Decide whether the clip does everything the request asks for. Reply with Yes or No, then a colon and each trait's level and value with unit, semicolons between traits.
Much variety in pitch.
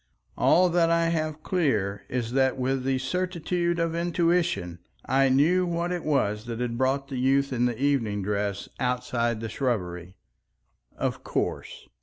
Yes: wide, 6.2 semitones